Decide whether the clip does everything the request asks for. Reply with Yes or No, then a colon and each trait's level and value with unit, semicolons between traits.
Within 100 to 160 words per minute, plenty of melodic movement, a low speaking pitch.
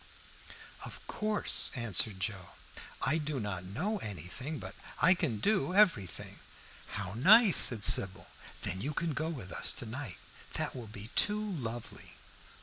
Yes: average, 145 wpm; wide, 8.7 semitones; low, 125 Hz